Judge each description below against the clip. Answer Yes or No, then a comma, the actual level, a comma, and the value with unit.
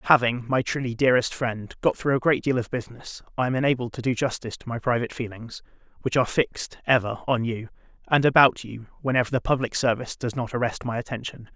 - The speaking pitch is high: No, low, 120 Hz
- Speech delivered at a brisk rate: Yes, fast, 210 wpm